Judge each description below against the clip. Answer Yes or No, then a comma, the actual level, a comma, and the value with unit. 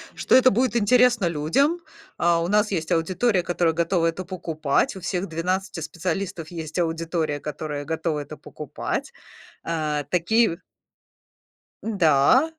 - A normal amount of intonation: Yes, average, 3.8 semitones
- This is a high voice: No, medium, 170 Hz